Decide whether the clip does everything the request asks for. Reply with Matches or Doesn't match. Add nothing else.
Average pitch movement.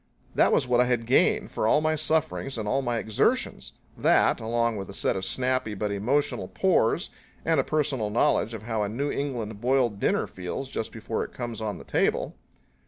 Matches